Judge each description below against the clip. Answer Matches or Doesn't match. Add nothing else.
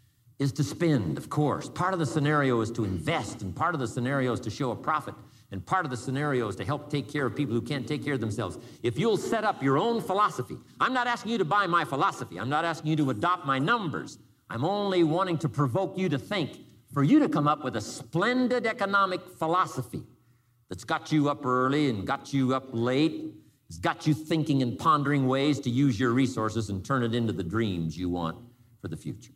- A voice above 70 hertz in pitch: Matches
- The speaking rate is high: Matches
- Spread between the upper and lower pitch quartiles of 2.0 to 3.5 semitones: Doesn't match